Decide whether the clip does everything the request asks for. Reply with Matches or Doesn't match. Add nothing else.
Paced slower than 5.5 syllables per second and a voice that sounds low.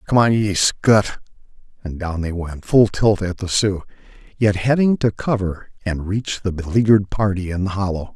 Matches